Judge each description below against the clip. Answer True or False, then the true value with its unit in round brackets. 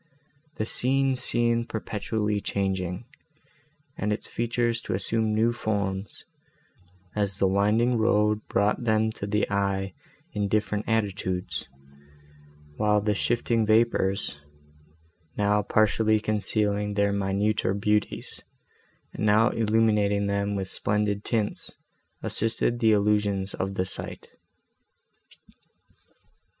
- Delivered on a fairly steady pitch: True (1.6 semitones)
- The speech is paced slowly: True (105 wpm)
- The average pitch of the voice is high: False (105 Hz)